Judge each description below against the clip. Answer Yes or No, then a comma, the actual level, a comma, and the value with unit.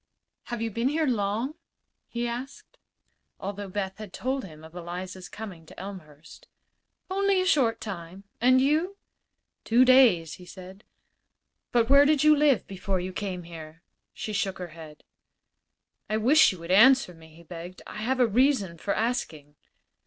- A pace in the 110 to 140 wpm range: No, average, 160 wpm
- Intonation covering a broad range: Yes, wide, 6.2 semitones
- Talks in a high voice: Yes, high, 205 Hz